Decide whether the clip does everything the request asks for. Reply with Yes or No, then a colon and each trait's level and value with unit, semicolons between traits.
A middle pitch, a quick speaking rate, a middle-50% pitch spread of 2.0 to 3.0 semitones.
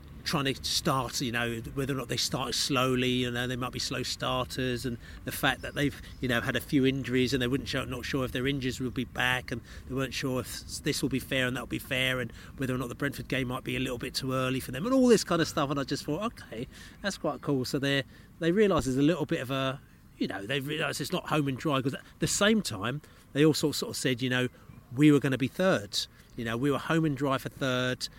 No: low, 130 Hz; fast, 285 wpm; narrow, 2.4 semitones